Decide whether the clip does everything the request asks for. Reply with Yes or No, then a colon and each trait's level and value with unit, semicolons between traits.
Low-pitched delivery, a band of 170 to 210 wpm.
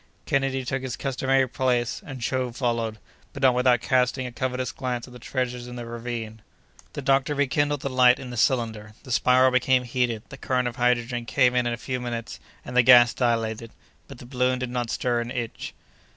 Yes: low, 125 Hz; average, 200 wpm